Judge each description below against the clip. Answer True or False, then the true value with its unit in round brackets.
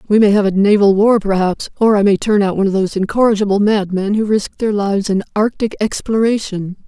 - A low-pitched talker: False (205 Hz)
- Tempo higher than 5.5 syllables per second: True (6.0 syllables/s)